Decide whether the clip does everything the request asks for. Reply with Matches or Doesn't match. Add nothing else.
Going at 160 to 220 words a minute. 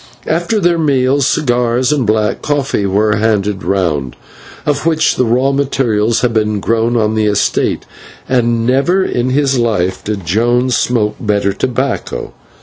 Doesn't match